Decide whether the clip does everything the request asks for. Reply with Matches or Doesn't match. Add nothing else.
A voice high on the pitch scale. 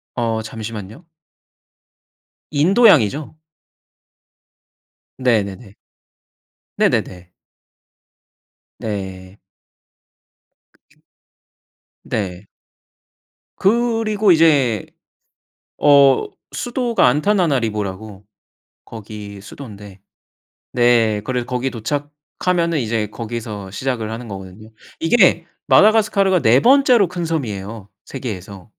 Doesn't match